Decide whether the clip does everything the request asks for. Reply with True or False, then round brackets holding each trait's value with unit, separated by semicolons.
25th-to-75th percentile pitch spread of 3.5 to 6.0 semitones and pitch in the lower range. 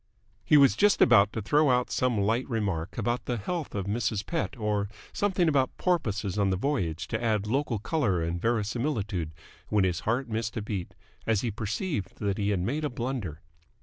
True (4.6 semitones; 110 Hz)